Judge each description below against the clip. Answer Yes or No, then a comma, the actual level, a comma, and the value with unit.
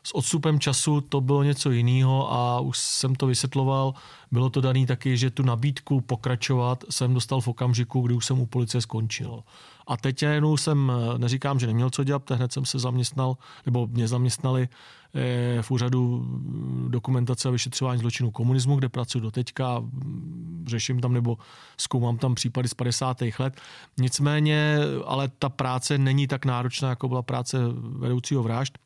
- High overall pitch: No, low, 130 Hz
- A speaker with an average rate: Yes, average, 160 wpm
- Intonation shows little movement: Yes, narrow, 1.8 semitones